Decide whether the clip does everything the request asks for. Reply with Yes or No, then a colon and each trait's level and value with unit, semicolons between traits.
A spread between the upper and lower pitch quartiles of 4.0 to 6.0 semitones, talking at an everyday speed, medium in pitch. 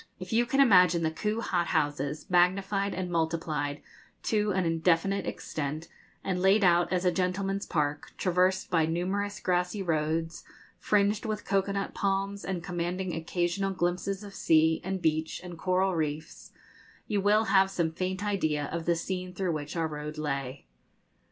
No: average, 3.2 semitones; average, 160 wpm; medium, 180 Hz